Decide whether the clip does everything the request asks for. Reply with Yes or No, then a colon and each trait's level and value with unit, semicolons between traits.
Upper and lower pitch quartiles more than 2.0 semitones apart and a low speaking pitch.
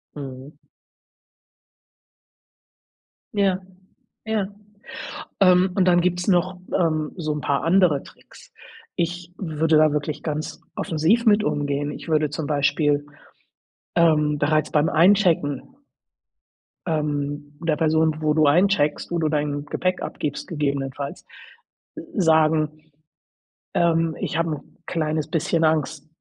No: average, 2.8 semitones; medium, 155 Hz